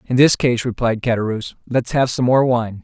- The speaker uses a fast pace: Yes, fast, 210 wpm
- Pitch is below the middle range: Yes, low, 120 Hz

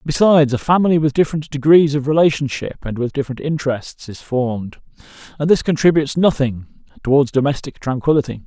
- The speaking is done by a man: Yes, male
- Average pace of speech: Yes, average, 150 wpm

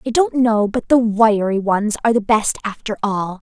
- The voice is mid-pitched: No, high, 220 Hz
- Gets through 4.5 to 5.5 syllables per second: Yes, 4.8 syllables/s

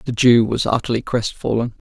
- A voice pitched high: No, low, 115 Hz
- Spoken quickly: No, average, 160 wpm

